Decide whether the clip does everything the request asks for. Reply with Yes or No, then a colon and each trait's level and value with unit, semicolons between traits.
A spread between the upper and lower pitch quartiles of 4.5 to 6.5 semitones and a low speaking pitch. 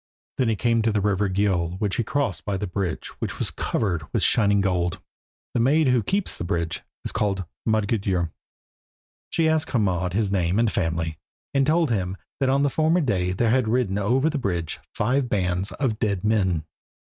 Yes: average, 5.2 semitones; low, 105 Hz